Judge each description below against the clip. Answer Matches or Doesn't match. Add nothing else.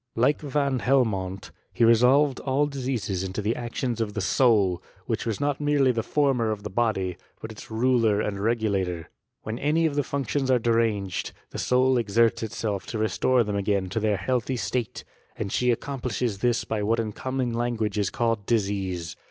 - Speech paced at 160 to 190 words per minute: Matches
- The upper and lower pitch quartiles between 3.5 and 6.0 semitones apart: Matches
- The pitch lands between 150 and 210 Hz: Doesn't match